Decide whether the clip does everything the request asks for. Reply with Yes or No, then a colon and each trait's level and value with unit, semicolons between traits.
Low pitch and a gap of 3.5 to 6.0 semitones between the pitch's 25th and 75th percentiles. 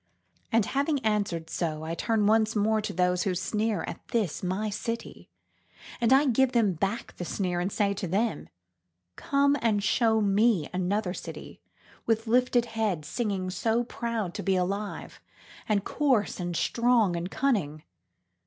No: high, 210 Hz; average, 4.2 semitones